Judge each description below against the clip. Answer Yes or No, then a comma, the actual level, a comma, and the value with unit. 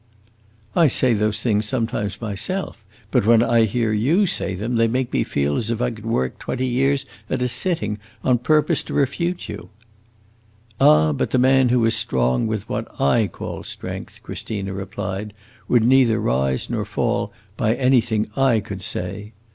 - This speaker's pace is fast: No, average, 170 wpm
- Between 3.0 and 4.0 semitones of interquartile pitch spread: Yes, average, 3.6 semitones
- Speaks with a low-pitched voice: Yes, low, 115 Hz